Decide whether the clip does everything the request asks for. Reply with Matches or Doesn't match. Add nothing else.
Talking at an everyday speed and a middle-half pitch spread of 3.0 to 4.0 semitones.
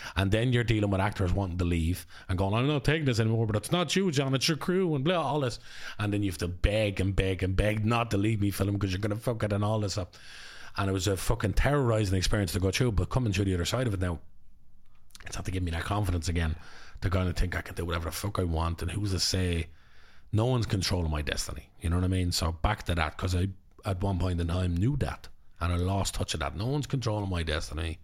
Doesn't match